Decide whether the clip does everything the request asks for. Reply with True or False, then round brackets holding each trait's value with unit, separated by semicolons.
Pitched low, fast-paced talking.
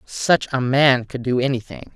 False (130 Hz; 185 wpm)